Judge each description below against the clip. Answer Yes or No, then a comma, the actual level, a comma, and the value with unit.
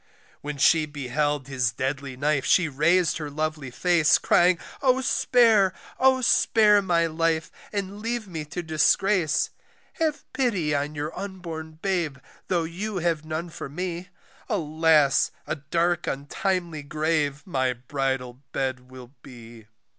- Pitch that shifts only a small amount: No, average, 4.4 semitones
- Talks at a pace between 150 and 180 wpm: No, slow, 135 wpm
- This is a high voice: No, medium, 160 Hz